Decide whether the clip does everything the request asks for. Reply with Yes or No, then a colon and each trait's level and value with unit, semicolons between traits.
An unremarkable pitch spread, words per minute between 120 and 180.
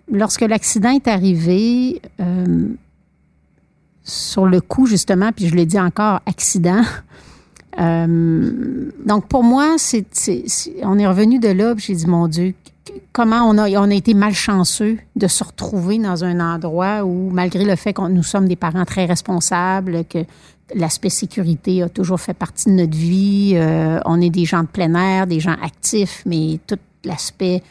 Yes: average, 3.3 semitones; average, 170 wpm